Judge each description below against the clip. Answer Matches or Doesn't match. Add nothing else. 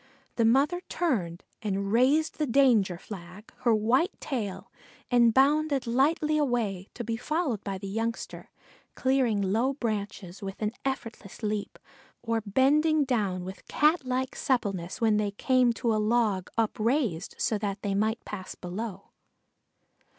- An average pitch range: Matches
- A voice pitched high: Matches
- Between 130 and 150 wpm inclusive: Matches